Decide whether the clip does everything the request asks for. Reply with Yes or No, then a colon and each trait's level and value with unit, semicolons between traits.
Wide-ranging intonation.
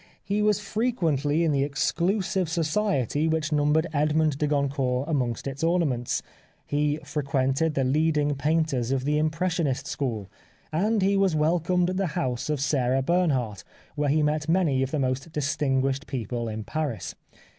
No: average, 3.4 semitones